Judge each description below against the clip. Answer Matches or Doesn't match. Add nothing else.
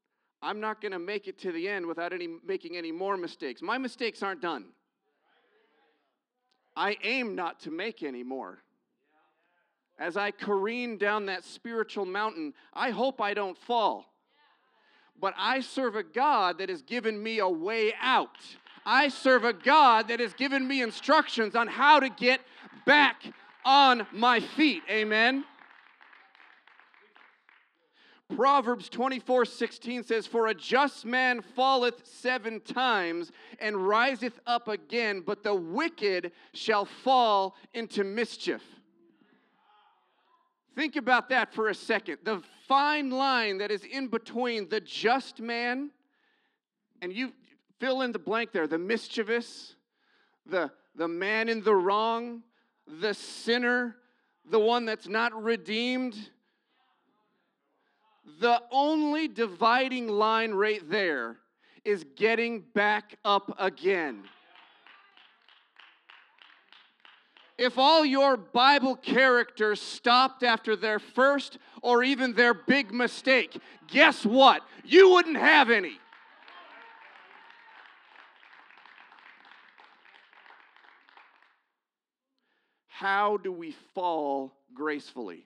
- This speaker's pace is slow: Matches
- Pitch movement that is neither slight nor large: Matches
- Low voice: Doesn't match